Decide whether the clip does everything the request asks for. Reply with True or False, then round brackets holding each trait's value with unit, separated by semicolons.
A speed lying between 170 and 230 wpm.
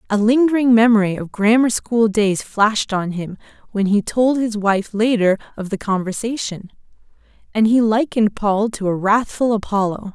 False (160 wpm)